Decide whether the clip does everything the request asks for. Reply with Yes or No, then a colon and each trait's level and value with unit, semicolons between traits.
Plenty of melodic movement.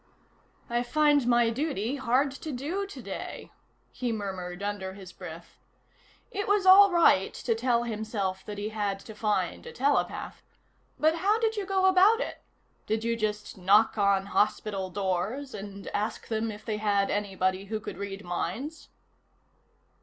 Yes: wide, 6.3 semitones